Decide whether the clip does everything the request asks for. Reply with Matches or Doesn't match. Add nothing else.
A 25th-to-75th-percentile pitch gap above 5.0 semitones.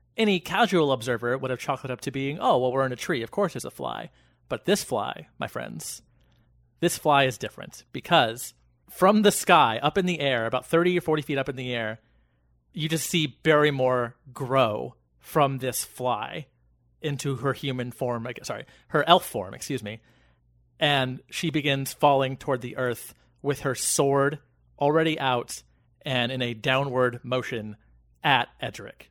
Doesn't match